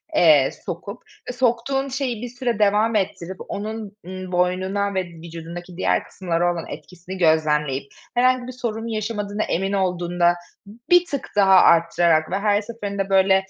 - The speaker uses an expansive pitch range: No, average, 4.2 semitones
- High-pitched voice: Yes, high, 195 Hz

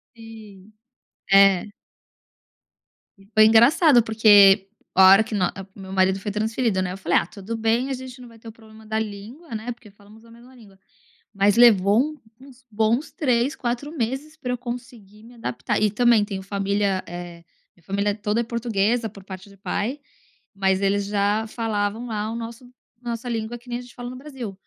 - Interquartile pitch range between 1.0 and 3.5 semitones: Yes, average, 3.2 semitones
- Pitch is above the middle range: Yes, high, 220 Hz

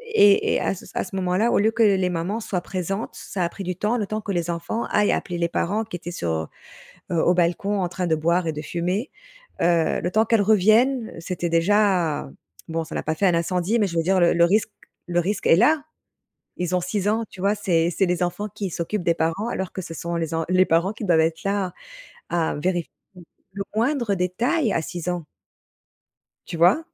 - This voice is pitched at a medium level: Yes, medium, 180 Hz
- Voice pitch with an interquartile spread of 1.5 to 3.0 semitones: No, average, 3.4 semitones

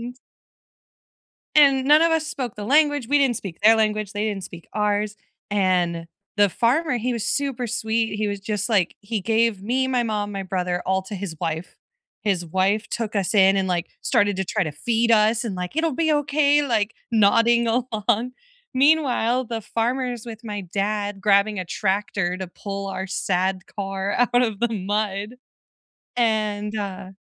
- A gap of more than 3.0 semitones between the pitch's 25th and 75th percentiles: Yes, average, 3.6 semitones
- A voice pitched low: No, high, 215 Hz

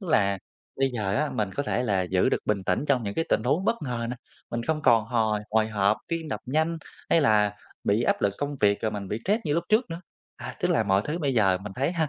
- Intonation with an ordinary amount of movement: No, wide, 6.6 semitones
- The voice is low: Yes, low, 115 Hz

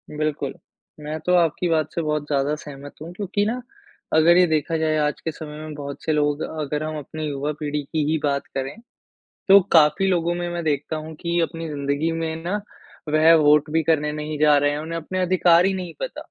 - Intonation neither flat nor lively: No, narrow, 2.1 semitones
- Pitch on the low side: No, medium, 155 Hz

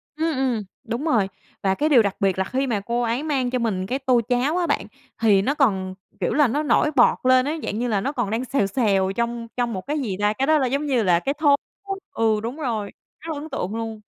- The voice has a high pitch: Yes, high, 240 Hz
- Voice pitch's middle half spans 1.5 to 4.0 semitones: No, average, 4.9 semitones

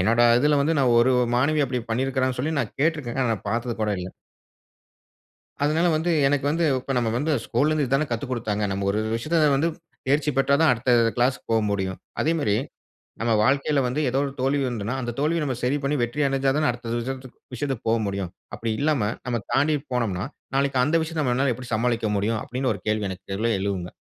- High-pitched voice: No, low, 130 Hz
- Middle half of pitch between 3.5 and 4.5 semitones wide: Yes, average, 4.1 semitones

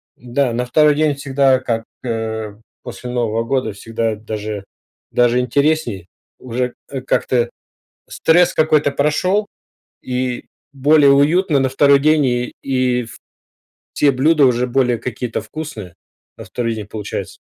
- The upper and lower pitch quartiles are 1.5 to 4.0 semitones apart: Yes, average, 3.6 semitones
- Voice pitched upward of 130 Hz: No, low, 125 Hz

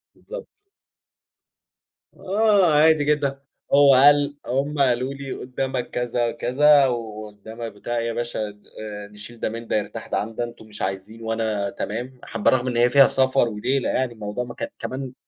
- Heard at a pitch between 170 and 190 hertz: No, low, 120 Hz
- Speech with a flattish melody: No, average, 3.7 semitones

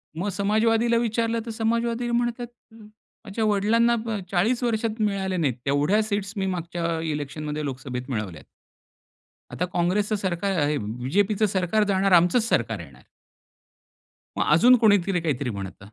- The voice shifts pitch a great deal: Yes, wide, 6.4 semitones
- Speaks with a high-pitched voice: Yes, high, 195 Hz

